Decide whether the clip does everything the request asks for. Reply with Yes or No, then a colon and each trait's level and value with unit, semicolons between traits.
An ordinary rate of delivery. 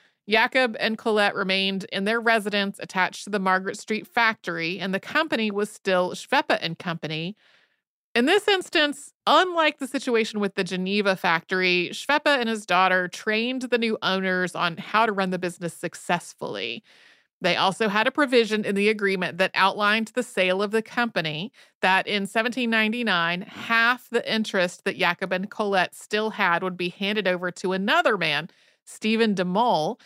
Yes: average, 165 wpm